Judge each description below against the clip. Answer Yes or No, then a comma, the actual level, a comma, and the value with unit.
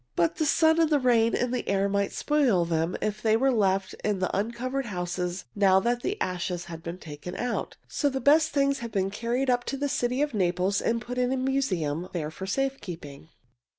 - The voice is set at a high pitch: Yes, high, 220 Hz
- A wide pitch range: Yes, wide, 6.5 semitones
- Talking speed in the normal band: No, fast, 220 wpm